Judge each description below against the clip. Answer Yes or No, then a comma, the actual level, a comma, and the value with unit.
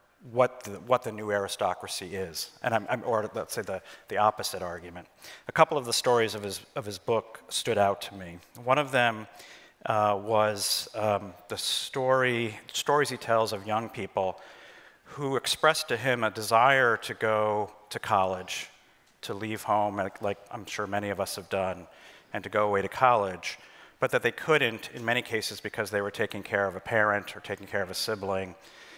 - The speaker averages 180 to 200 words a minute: Yes, average, 195 wpm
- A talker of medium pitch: No, low, 105 Hz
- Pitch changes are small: Yes, narrow, 2.2 semitones